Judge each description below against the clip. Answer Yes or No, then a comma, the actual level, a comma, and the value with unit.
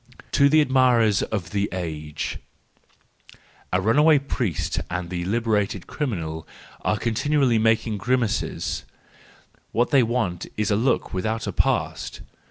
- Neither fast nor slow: No, slow, 125 wpm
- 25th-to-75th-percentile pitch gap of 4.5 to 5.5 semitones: Yes, average, 5.2 semitones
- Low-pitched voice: Yes, low, 110 Hz